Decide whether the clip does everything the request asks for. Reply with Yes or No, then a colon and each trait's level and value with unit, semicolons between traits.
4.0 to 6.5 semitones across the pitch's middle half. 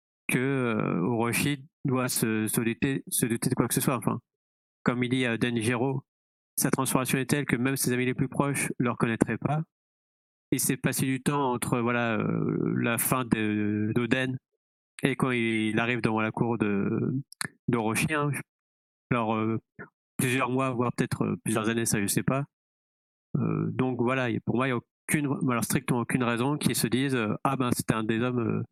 No: average, 3.1 semitones